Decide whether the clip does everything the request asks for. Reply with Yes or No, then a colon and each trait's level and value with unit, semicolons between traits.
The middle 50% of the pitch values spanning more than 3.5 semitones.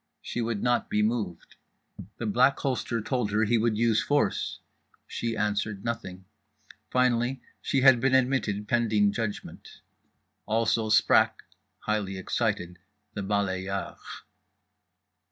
No: average, 2.8 semitones